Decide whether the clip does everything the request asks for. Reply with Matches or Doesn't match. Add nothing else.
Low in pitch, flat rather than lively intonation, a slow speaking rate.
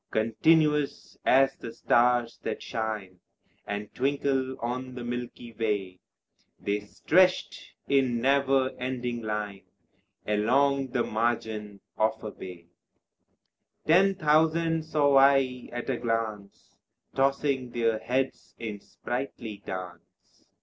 Doesn't match